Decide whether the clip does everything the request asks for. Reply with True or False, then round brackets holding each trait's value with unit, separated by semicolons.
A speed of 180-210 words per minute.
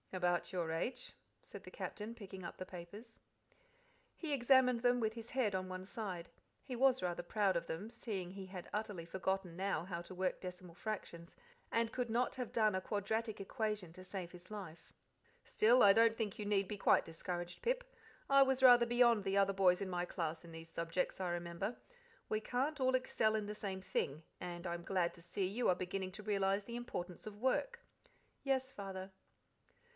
True (195 wpm)